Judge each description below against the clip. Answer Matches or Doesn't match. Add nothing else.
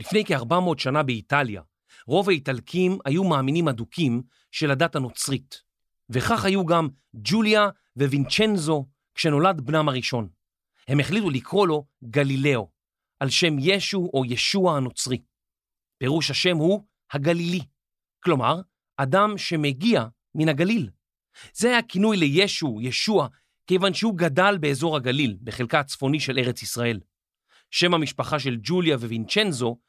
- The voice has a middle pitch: Matches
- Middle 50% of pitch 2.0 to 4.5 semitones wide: Doesn't match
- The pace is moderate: Matches